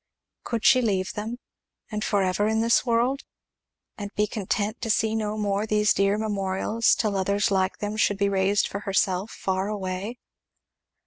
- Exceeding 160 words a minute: Yes, average, 170 wpm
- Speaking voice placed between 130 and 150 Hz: No, high, 205 Hz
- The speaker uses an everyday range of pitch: No, narrow, 1.9 semitones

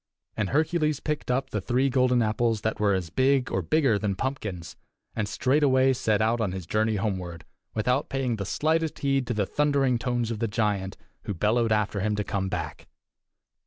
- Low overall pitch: Yes, low, 115 Hz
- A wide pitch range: No, average, 4.3 semitones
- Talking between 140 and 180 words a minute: No, average, 190 wpm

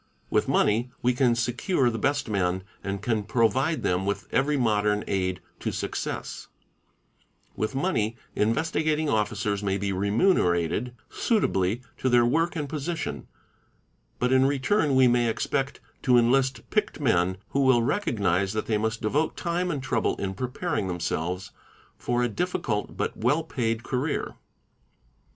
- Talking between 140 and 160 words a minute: Yes, average, 150 wpm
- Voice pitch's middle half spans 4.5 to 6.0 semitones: Yes, average, 5.2 semitones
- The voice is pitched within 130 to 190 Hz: No, low, 120 Hz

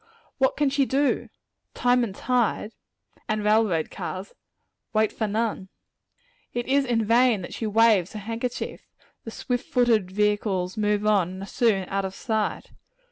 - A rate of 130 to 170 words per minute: Yes, average, 155 wpm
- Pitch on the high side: Yes, high, 215 Hz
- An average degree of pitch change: Yes, average, 3.2 semitones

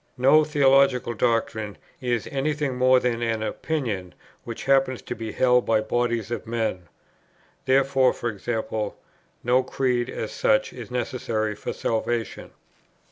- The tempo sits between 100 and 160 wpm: Yes, slow, 135 wpm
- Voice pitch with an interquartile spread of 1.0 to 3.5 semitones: Yes, average, 2.9 semitones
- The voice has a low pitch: Yes, low, 120 Hz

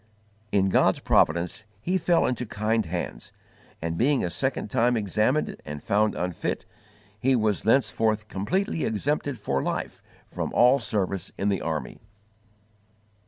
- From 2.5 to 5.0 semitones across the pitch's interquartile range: No, wide, 5.4 semitones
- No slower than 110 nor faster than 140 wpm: Yes, slow, 135 wpm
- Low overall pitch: Yes, low, 110 Hz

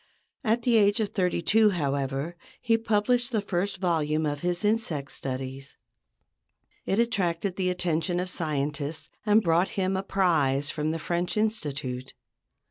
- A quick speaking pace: No, average, 145 wpm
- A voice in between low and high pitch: Yes, medium, 175 Hz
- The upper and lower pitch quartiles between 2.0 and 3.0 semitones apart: No, wide, 5.6 semitones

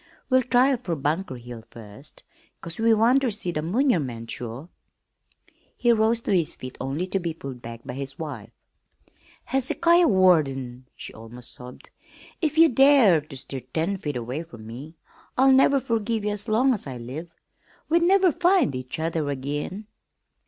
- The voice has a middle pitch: Yes, medium, 165 Hz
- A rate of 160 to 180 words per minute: Yes, average, 165 wpm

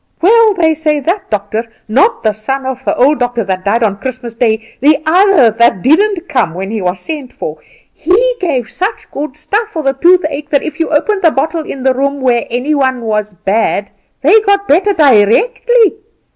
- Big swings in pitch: Yes, wide, 7.2 semitones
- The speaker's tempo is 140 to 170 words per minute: No, average, 195 wpm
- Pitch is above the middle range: Yes, very high, 275 Hz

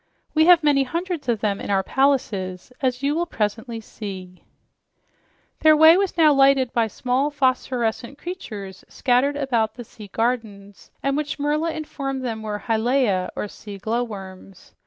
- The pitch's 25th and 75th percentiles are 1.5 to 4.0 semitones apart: No, average, 5.3 semitones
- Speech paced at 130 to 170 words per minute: Yes, average, 155 wpm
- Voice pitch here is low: No, very high, 250 Hz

